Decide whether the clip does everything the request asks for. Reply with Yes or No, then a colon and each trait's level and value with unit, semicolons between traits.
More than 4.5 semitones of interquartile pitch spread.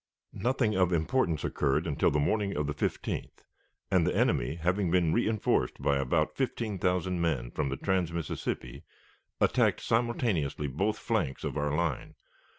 Yes: wide, 5.6 semitones